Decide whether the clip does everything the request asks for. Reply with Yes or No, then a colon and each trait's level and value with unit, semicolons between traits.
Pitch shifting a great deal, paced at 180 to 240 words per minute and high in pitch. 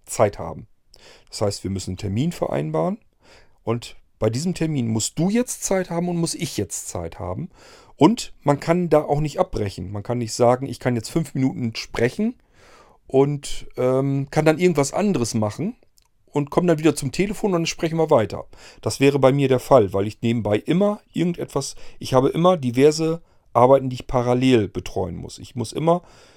No: wide, 6.1 semitones; fast, 190 wpm; low, 135 Hz